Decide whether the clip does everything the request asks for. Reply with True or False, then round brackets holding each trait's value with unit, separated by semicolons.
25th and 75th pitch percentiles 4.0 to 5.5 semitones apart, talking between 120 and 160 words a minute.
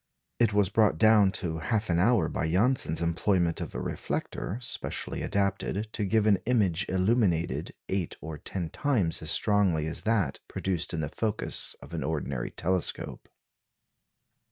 True (4.5 semitones; 155 wpm)